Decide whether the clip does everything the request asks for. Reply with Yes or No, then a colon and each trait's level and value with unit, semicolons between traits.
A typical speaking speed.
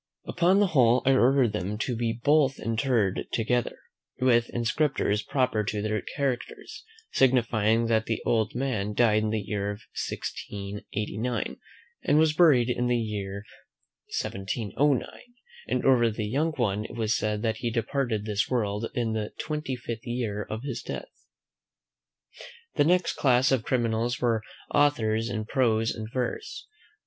Yes: average, 145 wpm